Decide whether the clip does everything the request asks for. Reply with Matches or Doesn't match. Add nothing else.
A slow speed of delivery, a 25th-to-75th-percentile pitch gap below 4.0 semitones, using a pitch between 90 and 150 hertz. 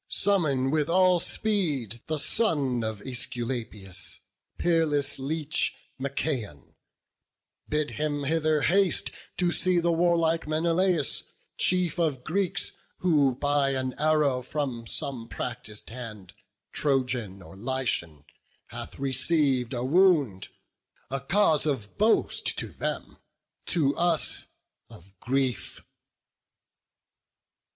Doesn't match